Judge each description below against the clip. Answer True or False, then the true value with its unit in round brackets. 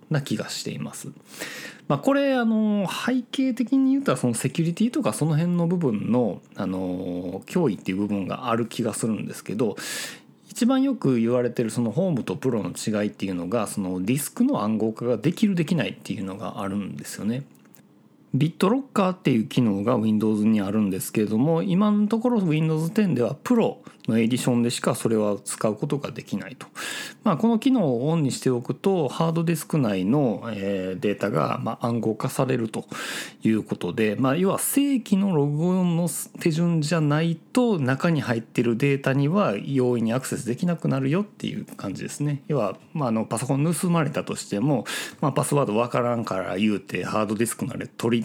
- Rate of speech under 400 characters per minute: False (405 characters per minute)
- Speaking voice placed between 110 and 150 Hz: True (140 Hz)